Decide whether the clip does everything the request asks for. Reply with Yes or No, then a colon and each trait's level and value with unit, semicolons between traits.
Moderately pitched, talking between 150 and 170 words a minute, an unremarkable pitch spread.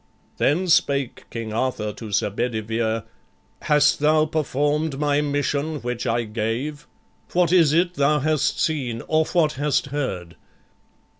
No: medium, 145 Hz; slow, 135 wpm; average, 4.8 semitones